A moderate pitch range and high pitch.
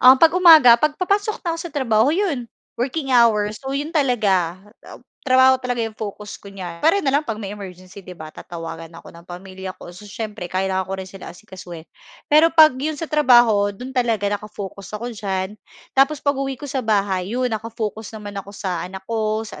No: wide, 5.8 semitones; high, 220 Hz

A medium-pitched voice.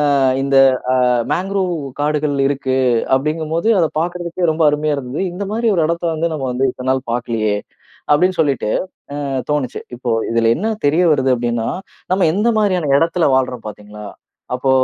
Yes: medium, 145 Hz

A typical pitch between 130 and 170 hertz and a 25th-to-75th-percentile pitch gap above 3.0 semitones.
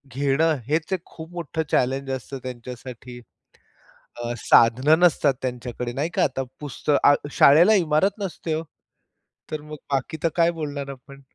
Yes: medium, 140 Hz; average, 3.8 semitones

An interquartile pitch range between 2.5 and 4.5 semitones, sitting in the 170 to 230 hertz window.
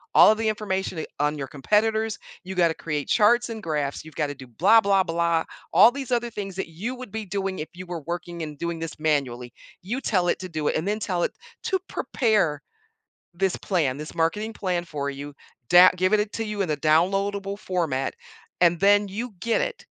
No: average, 4.9 semitones; medium, 185 Hz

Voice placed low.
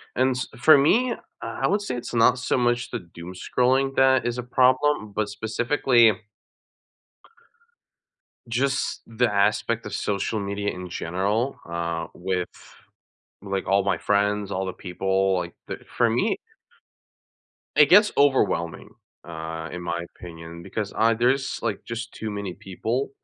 Yes: low, 110 Hz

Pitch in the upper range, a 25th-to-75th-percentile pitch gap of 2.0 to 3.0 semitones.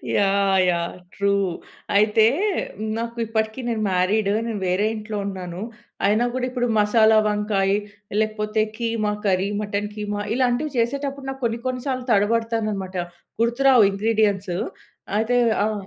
Yes: high, 215 Hz; narrow, 2.6 semitones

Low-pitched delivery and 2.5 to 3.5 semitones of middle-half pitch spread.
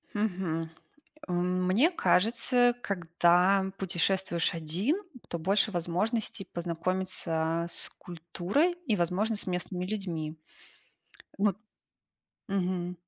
No: medium, 185 Hz; average, 2.9 semitones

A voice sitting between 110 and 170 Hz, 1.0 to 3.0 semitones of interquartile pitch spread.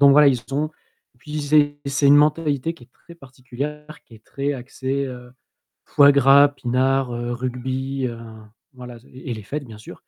Yes: low, 135 Hz; narrow, 2.6 semitones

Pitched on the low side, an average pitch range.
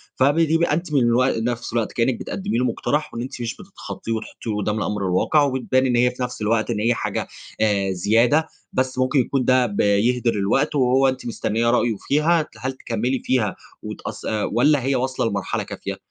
Yes: low, 125 Hz; average, 3.0 semitones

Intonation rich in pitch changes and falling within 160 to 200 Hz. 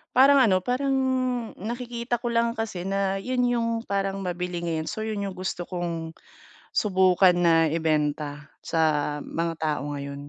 Yes: wide, 6.0 semitones; medium, 185 Hz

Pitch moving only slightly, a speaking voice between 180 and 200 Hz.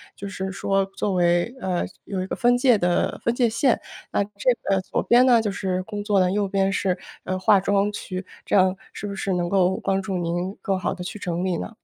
Yes: narrow, 2.0 semitones; high, 195 Hz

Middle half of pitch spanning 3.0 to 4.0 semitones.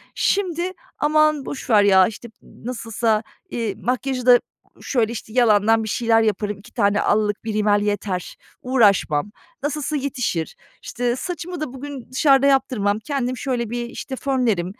No: average, 4.4 semitones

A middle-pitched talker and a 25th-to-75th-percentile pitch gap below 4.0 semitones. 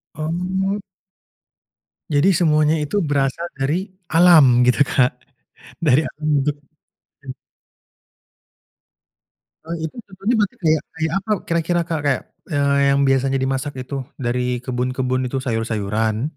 No: medium, 145 Hz; average, 4.3 semitones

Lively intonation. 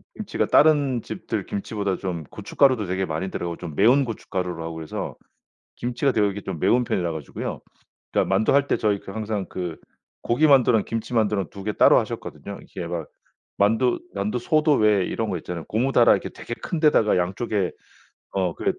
No: average, 4.7 semitones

